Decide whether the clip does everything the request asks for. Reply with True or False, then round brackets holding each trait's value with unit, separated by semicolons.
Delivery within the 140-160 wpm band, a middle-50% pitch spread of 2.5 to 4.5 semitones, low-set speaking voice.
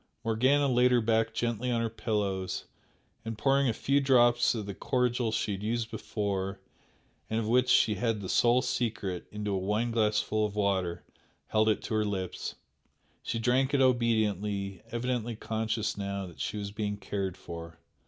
False (170 wpm; 2.9 semitones; 110 Hz)